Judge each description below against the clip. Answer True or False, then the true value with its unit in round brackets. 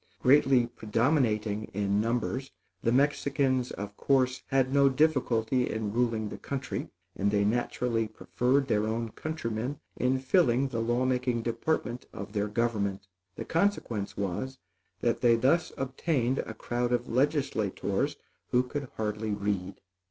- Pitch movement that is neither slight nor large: True (3.4 semitones)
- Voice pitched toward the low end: True (120 Hz)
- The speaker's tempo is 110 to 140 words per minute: True (135 wpm)